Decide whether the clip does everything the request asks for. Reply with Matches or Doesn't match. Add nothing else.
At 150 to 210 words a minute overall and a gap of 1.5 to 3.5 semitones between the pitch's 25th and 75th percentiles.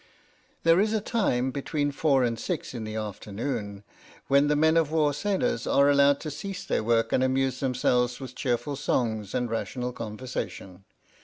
Doesn't match